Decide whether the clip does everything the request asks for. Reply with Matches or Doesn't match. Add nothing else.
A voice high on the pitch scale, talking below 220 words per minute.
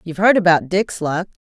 Doesn't match